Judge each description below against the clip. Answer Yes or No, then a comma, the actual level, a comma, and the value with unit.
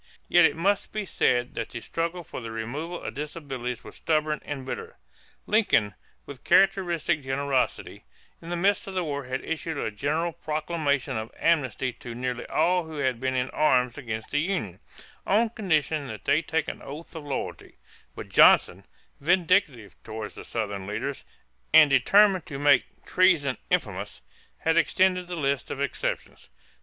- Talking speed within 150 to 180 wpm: Yes, average, 160 wpm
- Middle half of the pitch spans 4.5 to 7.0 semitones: Yes, average, 5.0 semitones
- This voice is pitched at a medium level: Yes, medium, 145 Hz